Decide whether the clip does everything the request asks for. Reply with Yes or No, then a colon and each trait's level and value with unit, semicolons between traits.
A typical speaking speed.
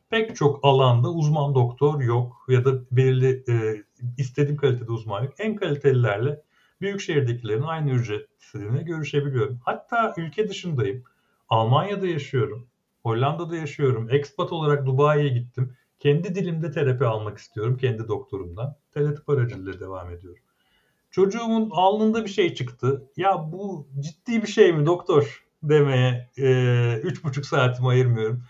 Yes: average, 130 wpm